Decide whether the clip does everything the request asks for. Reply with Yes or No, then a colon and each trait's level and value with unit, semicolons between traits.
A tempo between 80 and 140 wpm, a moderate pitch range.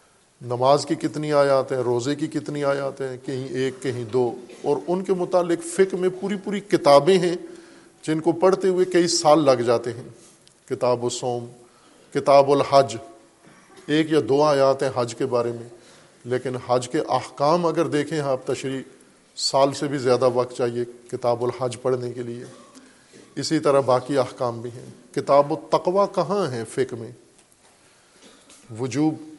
No: average, 160 wpm; average, 4.1 semitones